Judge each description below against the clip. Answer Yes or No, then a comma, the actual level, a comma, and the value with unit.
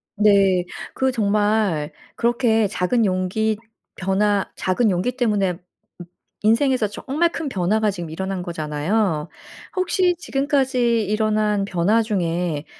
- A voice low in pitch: No, high, 210 Hz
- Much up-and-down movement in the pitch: No, average, 4.2 semitones